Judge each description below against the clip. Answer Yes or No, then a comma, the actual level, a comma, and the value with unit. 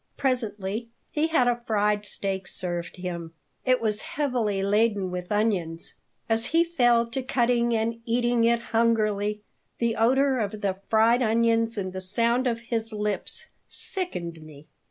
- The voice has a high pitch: Yes, high, 225 Hz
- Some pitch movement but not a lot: Yes, average, 3.1 semitones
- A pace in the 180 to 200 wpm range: No, average, 150 wpm